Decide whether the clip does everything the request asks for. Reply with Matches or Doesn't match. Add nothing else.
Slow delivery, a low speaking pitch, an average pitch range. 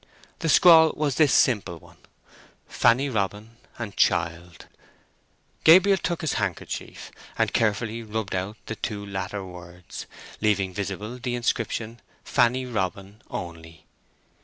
Matches